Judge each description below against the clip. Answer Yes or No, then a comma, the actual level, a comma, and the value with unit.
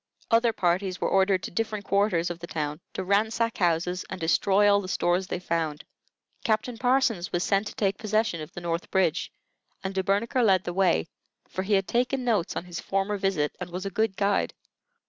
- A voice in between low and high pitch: No, high, 195 Hz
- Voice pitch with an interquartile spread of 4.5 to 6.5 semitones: No, average, 3.3 semitones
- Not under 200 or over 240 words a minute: Yes, fast, 205 wpm